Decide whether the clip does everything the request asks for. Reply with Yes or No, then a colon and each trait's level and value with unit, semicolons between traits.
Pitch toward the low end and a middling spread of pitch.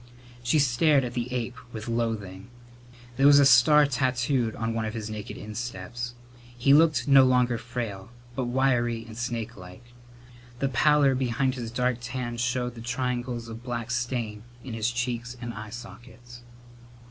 No: low, 120 Hz; narrow, 1.7 semitones